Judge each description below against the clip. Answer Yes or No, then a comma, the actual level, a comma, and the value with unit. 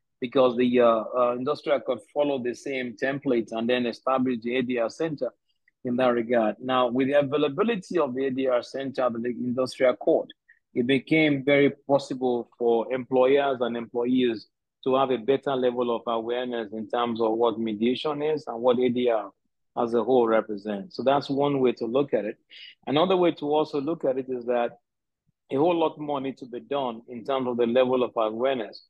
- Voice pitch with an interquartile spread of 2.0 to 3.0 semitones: Yes, narrow, 2.6 semitones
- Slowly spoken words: No, average, 185 wpm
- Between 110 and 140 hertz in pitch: Yes, low, 125 Hz